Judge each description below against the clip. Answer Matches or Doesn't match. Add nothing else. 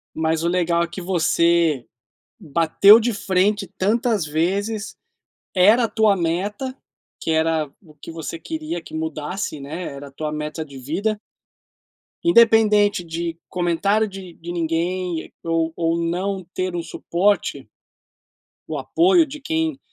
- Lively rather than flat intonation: Doesn't match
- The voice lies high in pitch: Doesn't match